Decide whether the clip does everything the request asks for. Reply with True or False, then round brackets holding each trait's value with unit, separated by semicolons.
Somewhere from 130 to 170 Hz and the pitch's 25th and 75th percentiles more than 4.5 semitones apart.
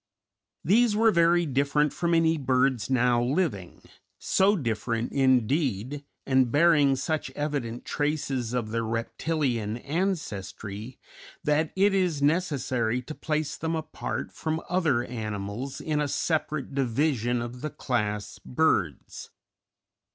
True (140 Hz; 5.0 semitones)